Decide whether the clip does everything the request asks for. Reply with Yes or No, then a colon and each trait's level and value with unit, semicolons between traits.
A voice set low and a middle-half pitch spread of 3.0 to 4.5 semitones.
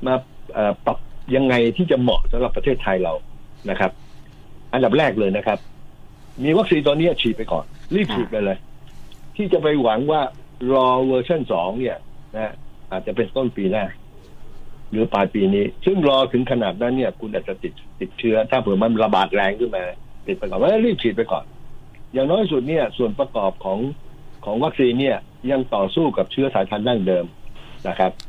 Yes: low, 125 Hz; average, 4.2 semitones